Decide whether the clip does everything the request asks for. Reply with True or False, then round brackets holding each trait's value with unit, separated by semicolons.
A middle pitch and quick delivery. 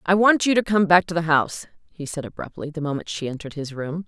True (165 Hz; 265 wpm)